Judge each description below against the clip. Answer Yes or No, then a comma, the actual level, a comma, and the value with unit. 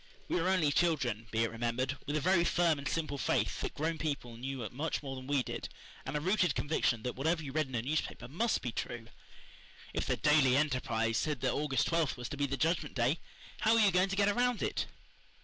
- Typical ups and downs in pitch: Yes, average, 4.4 semitones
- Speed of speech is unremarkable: No, fast, 230 wpm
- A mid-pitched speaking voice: Yes, medium, 145 Hz